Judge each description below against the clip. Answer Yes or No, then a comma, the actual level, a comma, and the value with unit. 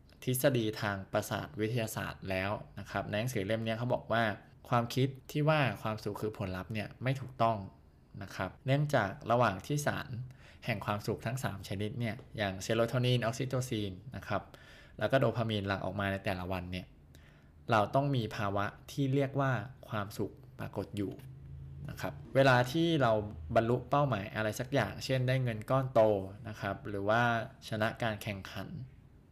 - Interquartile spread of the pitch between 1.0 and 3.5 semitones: No, average, 4.3 semitones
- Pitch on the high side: No, low, 110 Hz